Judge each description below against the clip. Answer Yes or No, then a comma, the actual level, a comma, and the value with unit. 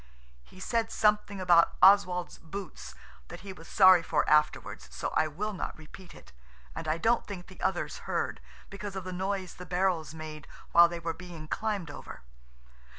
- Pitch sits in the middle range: Yes, medium, 180 Hz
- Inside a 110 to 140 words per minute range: No, average, 175 wpm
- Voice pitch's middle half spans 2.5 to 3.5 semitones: Yes, average, 3.2 semitones